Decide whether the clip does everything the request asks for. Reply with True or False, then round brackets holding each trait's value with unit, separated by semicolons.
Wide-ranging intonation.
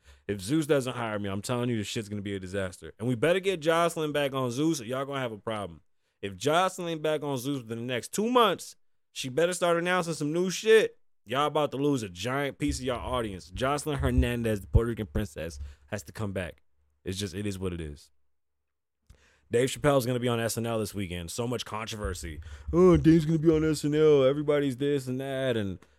True (7.2 semitones)